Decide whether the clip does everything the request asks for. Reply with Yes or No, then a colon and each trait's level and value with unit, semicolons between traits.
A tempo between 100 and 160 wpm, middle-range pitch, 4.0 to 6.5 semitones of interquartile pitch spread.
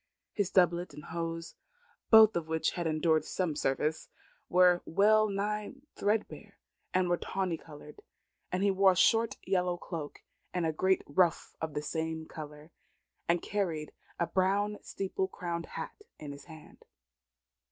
No: average, 145 wpm; medium, 175 Hz; average, 3.3 semitones